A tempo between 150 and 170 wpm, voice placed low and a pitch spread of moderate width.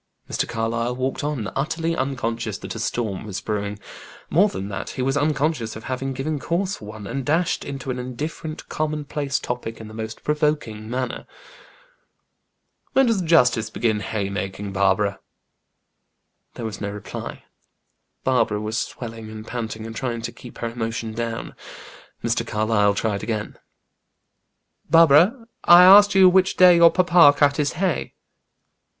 No: average, 155 wpm; low, 125 Hz; wide, 5.8 semitones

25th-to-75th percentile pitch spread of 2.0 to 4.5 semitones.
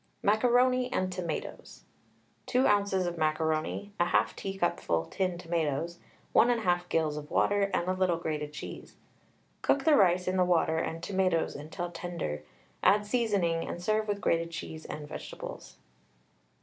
Yes: average, 3.7 semitones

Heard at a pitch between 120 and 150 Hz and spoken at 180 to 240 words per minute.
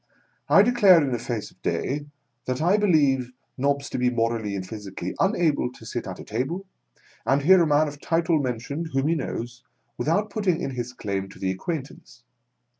Yes: medium, 140 Hz; average, 190 wpm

